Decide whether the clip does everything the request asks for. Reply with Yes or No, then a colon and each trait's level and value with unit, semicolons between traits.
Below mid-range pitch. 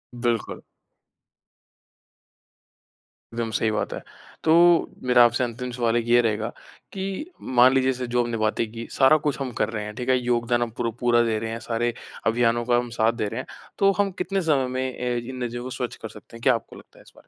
Yes: low, 120 Hz